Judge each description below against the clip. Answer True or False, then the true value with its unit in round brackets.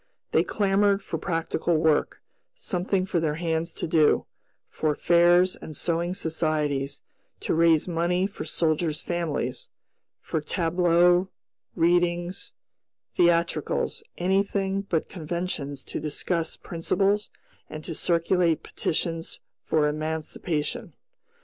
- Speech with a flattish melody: True (2.2 semitones)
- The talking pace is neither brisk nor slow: False (105 wpm)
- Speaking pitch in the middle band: True (170 Hz)